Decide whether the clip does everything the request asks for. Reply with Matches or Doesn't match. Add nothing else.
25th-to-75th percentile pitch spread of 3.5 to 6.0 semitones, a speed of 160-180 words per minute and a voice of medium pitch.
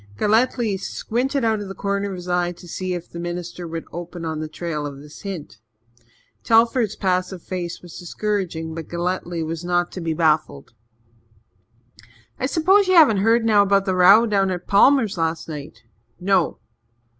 Matches